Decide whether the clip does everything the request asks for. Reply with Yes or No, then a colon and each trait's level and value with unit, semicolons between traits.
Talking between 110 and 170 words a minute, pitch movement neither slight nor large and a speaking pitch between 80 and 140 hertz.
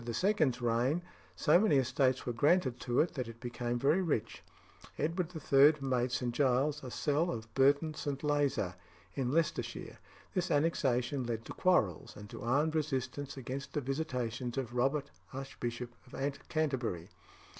Yes: average, 150 wpm; average, 3.7 semitones; low, 135 Hz